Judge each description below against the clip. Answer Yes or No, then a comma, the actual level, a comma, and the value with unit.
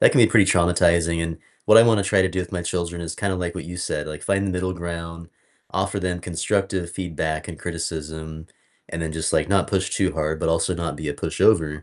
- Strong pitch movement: No, narrow, 2.6 semitones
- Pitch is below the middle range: Yes, very low, 85 Hz